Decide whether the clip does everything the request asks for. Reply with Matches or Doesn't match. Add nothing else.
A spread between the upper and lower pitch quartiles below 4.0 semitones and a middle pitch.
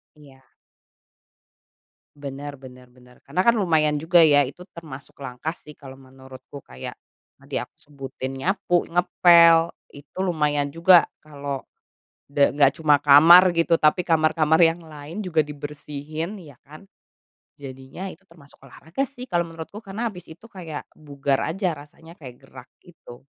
Matches